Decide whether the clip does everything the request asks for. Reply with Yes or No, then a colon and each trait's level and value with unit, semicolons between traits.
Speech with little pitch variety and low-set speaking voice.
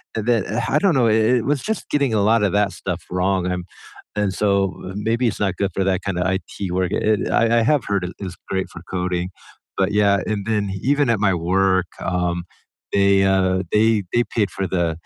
No: average, 3.1 semitones; low, 100 Hz